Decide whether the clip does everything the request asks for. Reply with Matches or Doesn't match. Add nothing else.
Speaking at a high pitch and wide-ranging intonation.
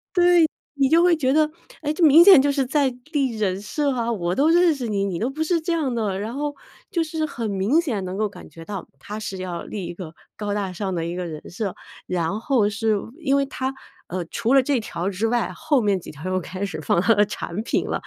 Matches